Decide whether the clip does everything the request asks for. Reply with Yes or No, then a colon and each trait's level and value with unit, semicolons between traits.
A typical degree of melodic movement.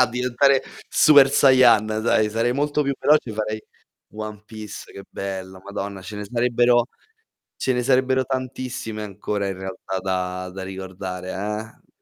Yes: average, 4.8 semitones